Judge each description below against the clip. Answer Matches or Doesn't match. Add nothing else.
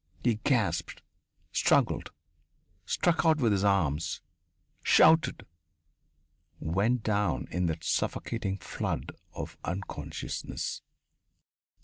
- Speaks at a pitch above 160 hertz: Doesn't match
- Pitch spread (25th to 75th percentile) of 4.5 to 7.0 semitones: Matches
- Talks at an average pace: Doesn't match